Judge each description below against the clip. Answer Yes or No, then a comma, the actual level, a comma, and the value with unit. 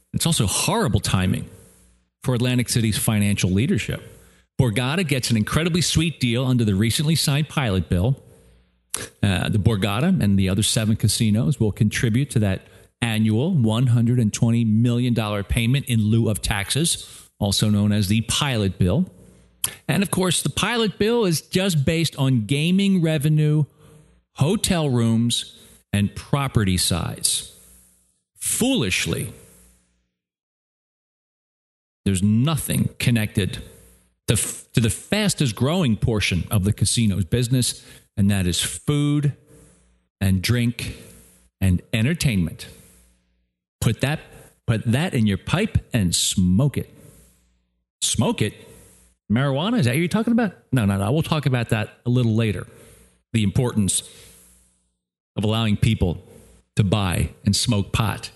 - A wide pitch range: Yes, wide, 5.8 semitones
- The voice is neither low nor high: No, low, 115 Hz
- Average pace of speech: No, slow, 130 wpm